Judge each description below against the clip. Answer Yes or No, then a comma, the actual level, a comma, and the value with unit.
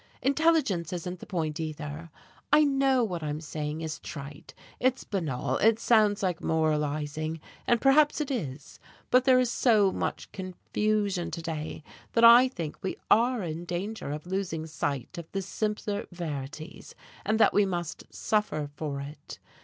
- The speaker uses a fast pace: No, average, 155 wpm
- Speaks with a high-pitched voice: No, medium, 175 Hz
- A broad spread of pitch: Yes, wide, 6.1 semitones